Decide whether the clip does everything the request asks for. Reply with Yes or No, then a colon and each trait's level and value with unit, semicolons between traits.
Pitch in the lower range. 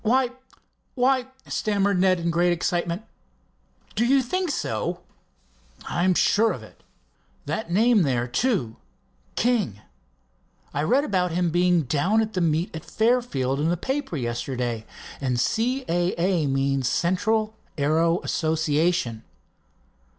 No: medium, 175 Hz